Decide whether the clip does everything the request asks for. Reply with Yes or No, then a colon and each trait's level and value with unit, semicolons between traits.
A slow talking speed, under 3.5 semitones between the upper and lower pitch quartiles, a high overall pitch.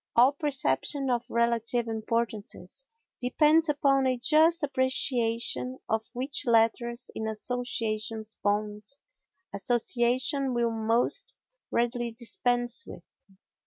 Yes: slow, 95 wpm; narrow, 2.6 semitones; high, 240 Hz